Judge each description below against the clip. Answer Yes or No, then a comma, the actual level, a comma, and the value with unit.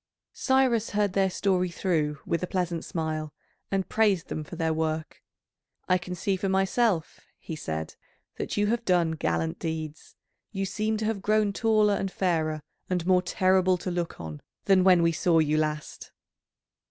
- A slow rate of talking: No, average, 170 wpm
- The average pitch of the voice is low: No, medium, 180 Hz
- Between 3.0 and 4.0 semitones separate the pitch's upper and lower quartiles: Yes, average, 3.6 semitones